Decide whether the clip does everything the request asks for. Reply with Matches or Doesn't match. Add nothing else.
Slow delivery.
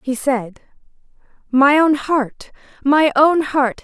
Matches